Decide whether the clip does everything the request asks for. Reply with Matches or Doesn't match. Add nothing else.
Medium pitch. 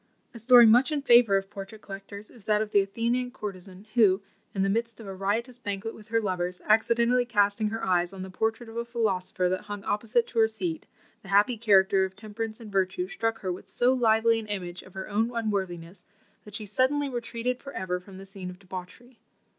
Doesn't match